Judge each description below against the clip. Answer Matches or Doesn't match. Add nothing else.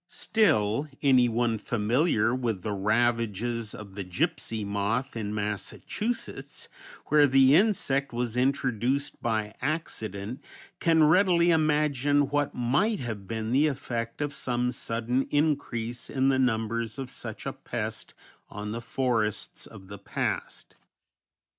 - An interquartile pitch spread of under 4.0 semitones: Doesn't match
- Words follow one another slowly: Matches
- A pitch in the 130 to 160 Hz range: Doesn't match